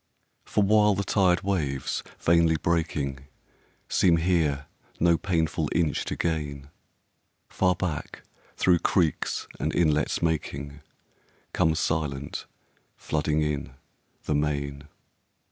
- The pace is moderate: No, slow, 95 wpm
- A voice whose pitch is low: Yes, very low, 80 Hz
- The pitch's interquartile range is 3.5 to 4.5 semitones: No, average, 3.0 semitones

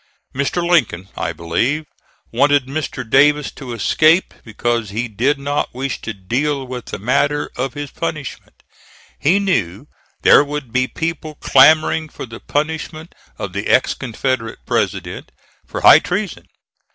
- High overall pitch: No, low, 135 Hz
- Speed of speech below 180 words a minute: Yes, average, 140 wpm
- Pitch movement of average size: Yes, average, 4.2 semitones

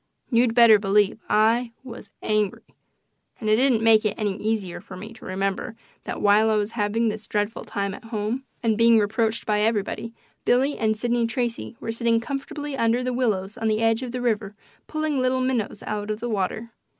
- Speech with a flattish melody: Yes, narrow, 2.3 semitones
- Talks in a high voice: Yes, high, 225 Hz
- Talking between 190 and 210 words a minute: Yes, average, 195 wpm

